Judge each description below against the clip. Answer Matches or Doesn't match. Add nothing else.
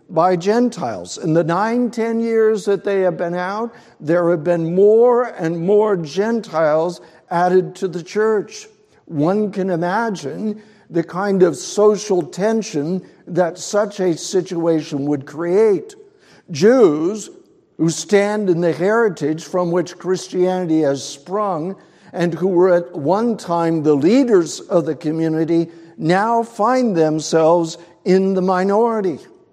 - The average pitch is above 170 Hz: Matches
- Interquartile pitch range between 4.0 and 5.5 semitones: Matches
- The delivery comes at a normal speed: Doesn't match